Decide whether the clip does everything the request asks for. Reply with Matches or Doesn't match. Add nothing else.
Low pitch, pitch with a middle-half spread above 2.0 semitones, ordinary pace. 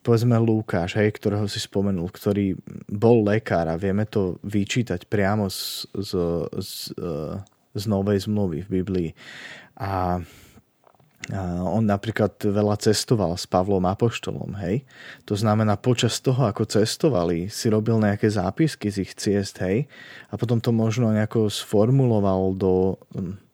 Matches